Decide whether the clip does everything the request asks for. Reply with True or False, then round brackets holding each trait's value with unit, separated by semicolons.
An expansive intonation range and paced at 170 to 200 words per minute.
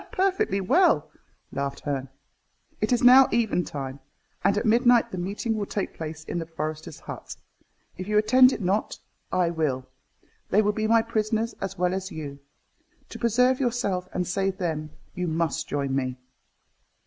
False (6.1 semitones; 160 wpm)